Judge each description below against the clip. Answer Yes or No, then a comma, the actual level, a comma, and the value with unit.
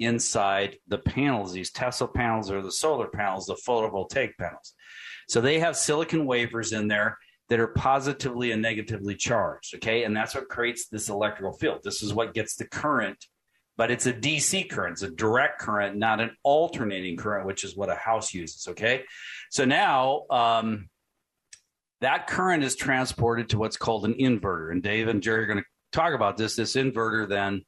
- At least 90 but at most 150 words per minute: No, average, 185 wpm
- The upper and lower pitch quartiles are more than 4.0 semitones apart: No, average, 2.8 semitones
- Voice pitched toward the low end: Yes, low, 110 Hz